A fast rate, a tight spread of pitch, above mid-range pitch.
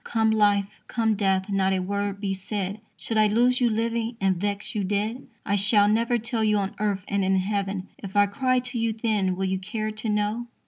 Yes: fast, 220 wpm; narrow, 2.2 semitones; high, 205 Hz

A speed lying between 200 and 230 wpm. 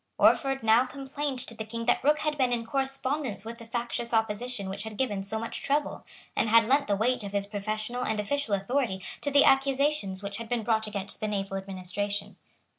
Yes: fast, 205 wpm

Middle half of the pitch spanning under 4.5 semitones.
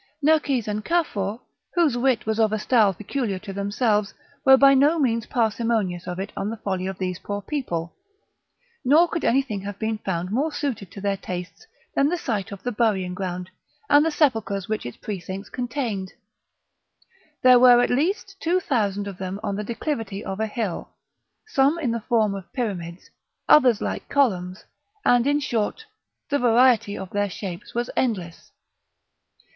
No: average, 4.9 semitones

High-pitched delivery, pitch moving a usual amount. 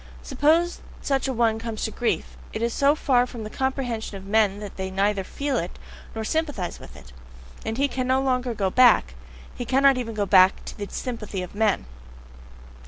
Yes: high, 230 Hz; average, 4.5 semitones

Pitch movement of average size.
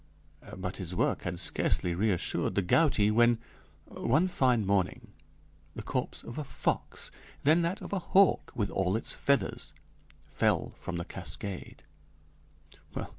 No: wide, 7.8 semitones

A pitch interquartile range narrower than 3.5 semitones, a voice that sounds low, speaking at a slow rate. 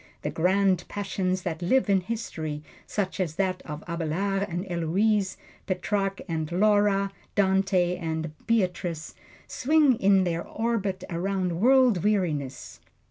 No: average, 2.9 semitones; high, 190 Hz; slow, 125 wpm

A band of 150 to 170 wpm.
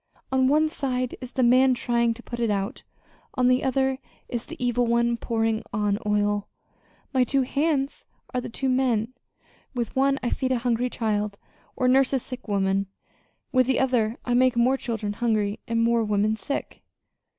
No: average, 180 wpm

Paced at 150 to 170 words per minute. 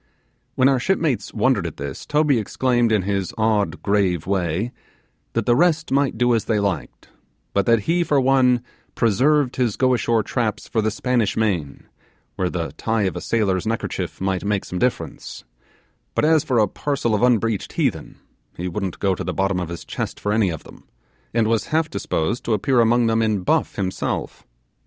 No: average, 190 wpm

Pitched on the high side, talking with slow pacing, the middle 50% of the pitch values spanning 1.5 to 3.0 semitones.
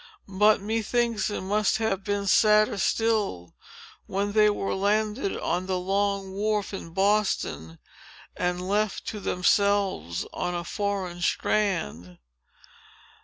Yes: high, 200 Hz; slow, 120 wpm; narrow, 2.5 semitones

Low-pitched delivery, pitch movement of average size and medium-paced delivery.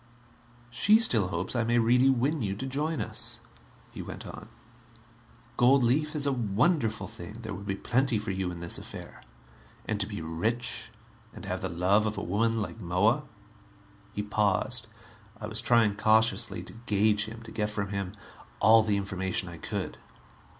Yes: low, 110 Hz; average, 3.3 semitones; average, 175 wpm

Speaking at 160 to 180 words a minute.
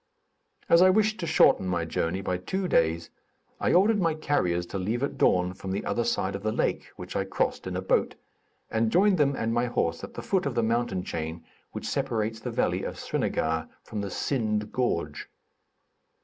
No: average, 200 wpm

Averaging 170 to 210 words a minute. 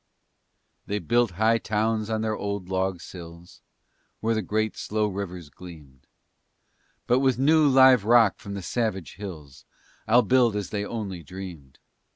No: average, 150 wpm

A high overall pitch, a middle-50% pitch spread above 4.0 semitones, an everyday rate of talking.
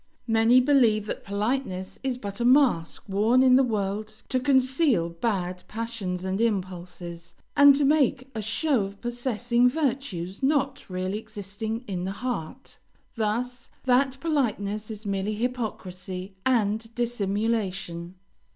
No: high, 220 Hz; average, 4.6 semitones; slow, 130 wpm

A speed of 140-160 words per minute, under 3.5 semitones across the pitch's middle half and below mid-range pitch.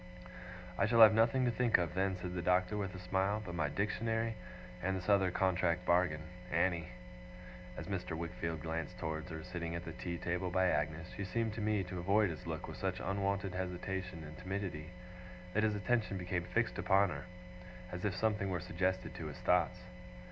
No: average, 190 wpm; narrow, 2.5 semitones; very low, 90 Hz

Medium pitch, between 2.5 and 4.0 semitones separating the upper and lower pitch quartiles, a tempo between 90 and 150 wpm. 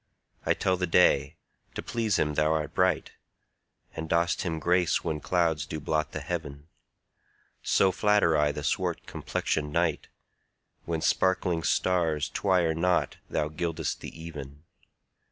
No: very low, 80 Hz; average, 2.8 semitones; average, 140 wpm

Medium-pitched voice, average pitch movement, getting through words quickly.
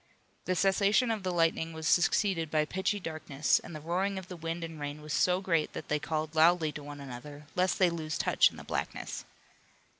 Yes: medium, 165 Hz; average, 3.1 semitones; fast, 210 wpm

